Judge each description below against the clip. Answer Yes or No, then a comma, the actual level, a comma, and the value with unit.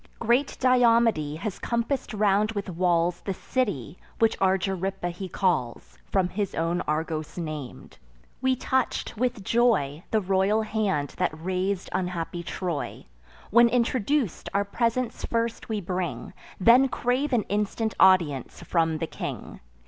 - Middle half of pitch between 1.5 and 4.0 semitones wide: No, average, 5.0 semitones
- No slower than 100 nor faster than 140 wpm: Yes, slow, 135 wpm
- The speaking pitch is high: Yes, high, 195 Hz